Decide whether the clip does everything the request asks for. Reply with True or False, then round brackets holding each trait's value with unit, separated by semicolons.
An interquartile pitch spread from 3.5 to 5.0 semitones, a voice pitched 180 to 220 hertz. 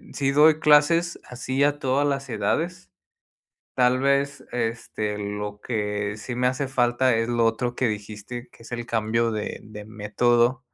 False (3.9 semitones; 120 Hz)